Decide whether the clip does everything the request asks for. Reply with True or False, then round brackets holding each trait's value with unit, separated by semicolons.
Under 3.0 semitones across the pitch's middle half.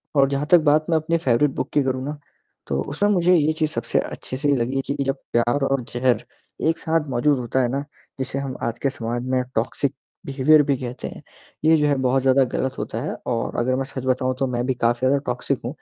True (2.6 semitones)